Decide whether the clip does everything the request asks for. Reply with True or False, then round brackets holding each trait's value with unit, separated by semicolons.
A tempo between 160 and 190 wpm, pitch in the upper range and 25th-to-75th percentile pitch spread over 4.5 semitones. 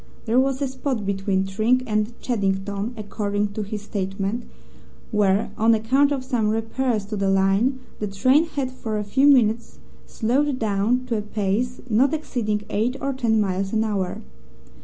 False (165 wpm; 220 Hz; 3.9 semitones)